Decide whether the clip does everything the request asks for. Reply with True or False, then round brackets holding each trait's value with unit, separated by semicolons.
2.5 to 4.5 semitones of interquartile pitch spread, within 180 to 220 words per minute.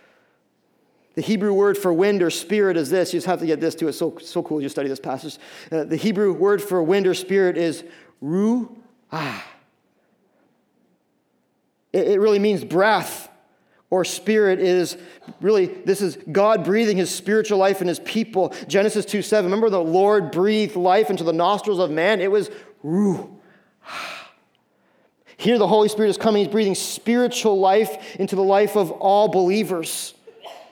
False (3.2 semitones; 170 wpm)